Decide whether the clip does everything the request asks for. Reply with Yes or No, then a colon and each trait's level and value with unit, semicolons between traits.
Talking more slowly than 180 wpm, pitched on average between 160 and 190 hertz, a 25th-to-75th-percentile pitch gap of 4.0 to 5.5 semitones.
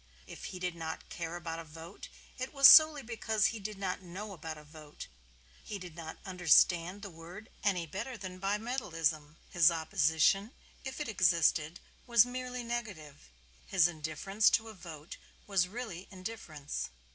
Yes: average, 155 wpm; medium, 185 Hz; average, 4.9 semitones